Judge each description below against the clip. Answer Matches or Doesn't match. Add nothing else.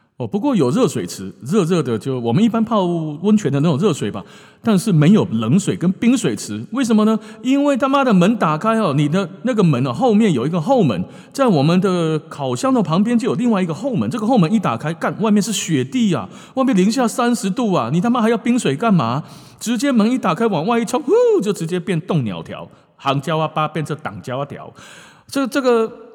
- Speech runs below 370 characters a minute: Matches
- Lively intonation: Matches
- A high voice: Matches